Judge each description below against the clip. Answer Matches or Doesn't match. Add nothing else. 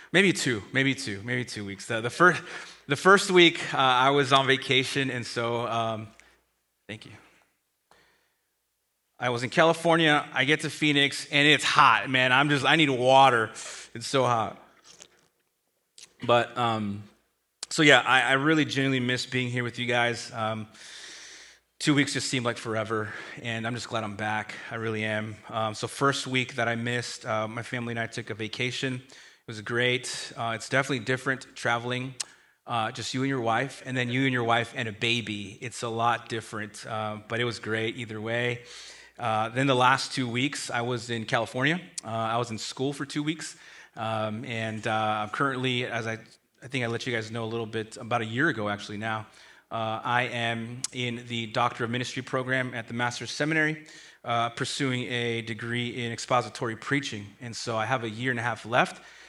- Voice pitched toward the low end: Matches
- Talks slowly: Doesn't match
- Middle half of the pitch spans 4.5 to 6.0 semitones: Doesn't match